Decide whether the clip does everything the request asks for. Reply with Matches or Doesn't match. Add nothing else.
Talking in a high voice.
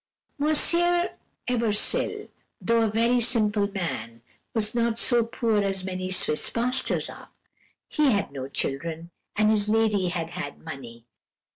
Matches